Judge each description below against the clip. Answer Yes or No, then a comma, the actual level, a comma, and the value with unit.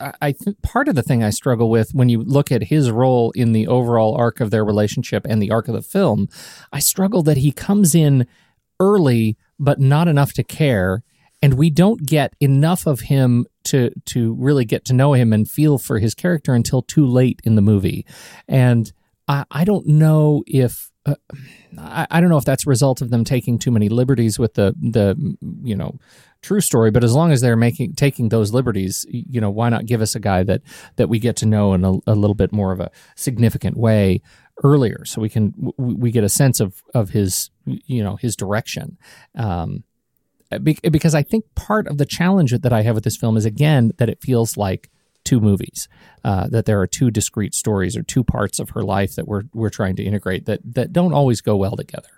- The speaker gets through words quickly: Yes, fast, 215 wpm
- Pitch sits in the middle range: No, low, 120 Hz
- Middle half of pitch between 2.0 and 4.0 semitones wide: No, average, 4.7 semitones